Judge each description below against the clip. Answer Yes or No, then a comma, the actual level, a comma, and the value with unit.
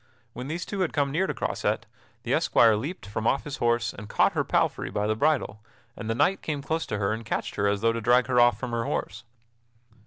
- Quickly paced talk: Yes, fast, 245 wpm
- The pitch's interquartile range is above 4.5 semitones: Yes, average, 4.9 semitones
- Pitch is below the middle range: Yes, low, 120 Hz